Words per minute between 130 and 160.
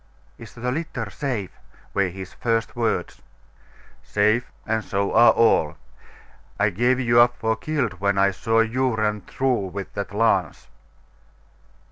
Yes: average, 140 wpm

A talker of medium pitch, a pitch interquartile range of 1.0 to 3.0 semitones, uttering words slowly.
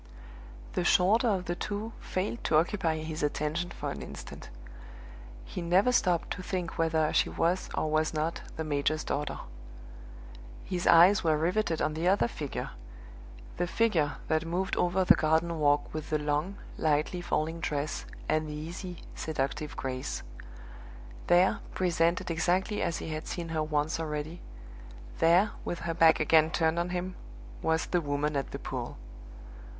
No: medium, 165 Hz; narrow, 2.6 semitones; average, 155 wpm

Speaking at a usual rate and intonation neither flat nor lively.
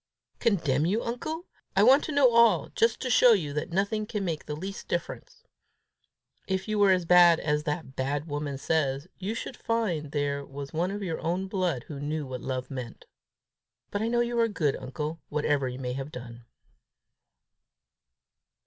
No: average, 180 wpm; wide, 6.5 semitones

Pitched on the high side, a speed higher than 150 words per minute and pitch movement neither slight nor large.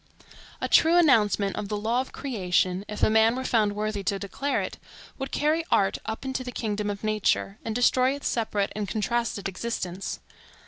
Yes: high, 215 Hz; average, 185 wpm; average, 3.9 semitones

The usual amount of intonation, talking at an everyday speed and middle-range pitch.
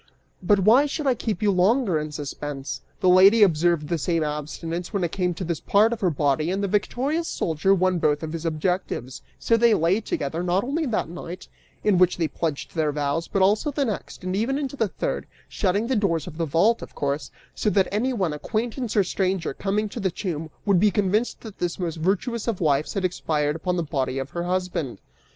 No: average, 4.6 semitones; fast, 215 wpm; medium, 180 Hz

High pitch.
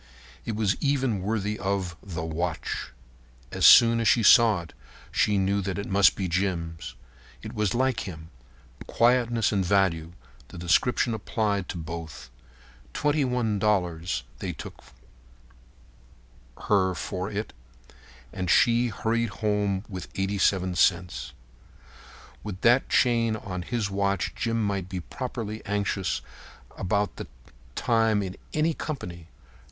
No: low, 100 Hz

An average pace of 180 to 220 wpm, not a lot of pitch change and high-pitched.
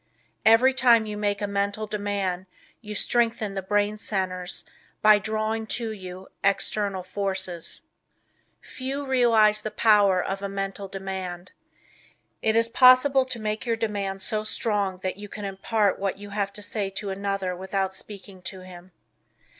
No: average, 155 wpm; narrow, 2.1 semitones; high, 205 Hz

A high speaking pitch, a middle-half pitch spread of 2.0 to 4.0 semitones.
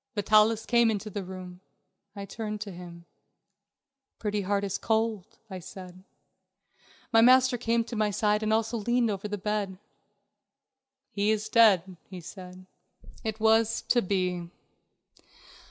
Yes: high, 210 Hz; average, 2.9 semitones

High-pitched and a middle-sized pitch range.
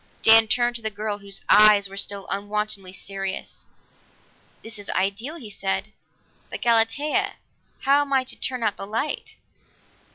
Yes: high, 215 Hz; average, 3.2 semitones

